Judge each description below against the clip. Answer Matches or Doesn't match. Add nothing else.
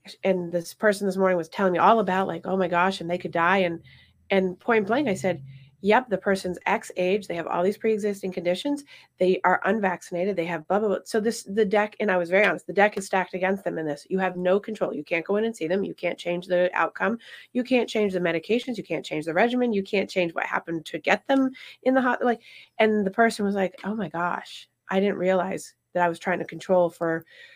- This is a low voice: Doesn't match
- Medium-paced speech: Doesn't match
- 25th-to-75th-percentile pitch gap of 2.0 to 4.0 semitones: Matches